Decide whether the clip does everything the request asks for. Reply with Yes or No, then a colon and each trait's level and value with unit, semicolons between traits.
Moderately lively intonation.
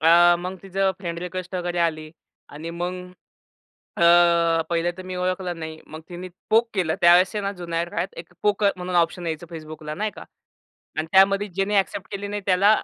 No: narrow, 2.3 semitones